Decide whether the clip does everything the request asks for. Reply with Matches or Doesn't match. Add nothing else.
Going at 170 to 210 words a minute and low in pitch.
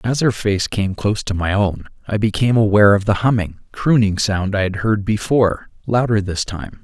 Matches